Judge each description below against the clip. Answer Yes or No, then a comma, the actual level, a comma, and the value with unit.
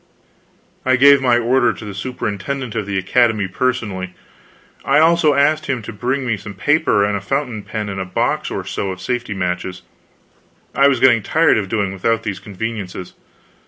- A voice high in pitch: No, low, 115 Hz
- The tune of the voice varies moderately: Yes, average, 4.8 semitones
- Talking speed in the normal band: Yes, average, 180 wpm